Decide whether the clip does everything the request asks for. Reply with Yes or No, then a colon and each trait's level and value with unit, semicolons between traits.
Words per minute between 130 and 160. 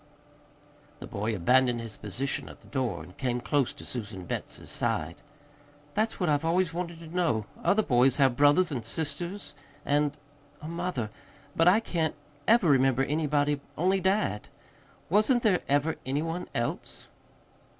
Yes: average, 150 wpm